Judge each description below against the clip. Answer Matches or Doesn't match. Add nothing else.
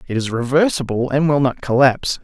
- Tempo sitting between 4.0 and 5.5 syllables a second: Doesn't match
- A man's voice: Matches